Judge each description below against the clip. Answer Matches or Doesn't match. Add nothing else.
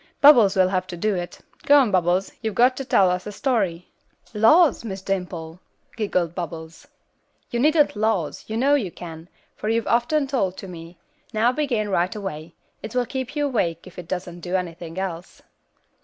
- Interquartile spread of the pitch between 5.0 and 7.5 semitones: Matches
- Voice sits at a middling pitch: Doesn't match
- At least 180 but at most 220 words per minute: Matches